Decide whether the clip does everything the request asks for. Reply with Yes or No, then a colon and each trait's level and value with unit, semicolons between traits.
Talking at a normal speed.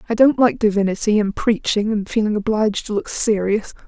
Yes: average, 185 wpm